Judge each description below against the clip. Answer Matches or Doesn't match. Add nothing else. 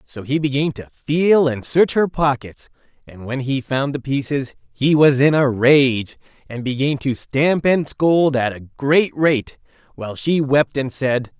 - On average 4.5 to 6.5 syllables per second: Doesn't match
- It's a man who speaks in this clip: Matches